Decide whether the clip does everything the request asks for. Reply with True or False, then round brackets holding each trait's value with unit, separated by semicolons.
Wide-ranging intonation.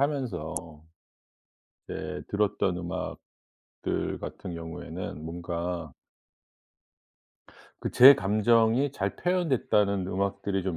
False (4.9 semitones)